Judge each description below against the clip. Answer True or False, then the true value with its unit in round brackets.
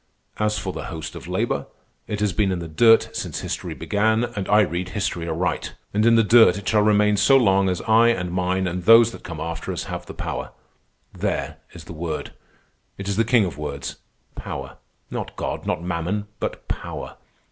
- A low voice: True (95 Hz)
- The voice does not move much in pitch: False (3.9 semitones)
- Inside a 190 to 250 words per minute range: True (200 wpm)